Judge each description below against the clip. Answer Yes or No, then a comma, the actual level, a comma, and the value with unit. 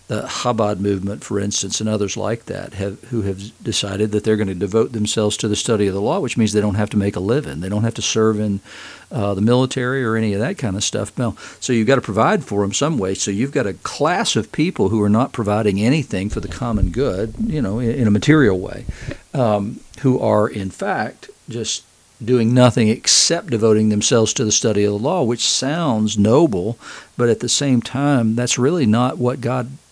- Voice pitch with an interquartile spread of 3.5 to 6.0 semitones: No, average, 3.0 semitones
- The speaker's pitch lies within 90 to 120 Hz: Yes, low, 110 Hz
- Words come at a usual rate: No, fast, 225 wpm